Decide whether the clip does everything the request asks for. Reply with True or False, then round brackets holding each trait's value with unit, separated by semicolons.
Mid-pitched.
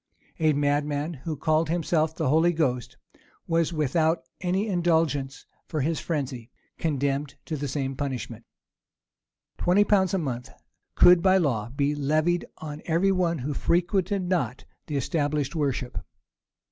True (155 Hz)